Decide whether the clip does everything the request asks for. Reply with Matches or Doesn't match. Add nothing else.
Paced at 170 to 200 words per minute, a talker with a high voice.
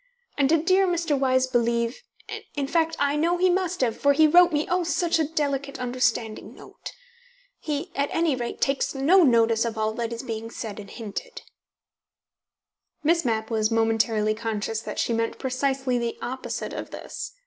Matches